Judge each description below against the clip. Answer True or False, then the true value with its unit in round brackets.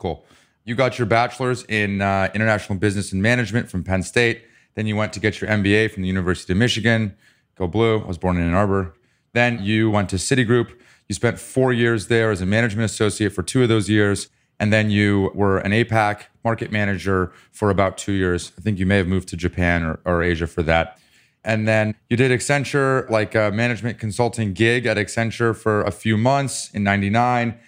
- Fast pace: True (210 wpm)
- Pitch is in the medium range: False (105 Hz)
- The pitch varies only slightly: False (3.2 semitones)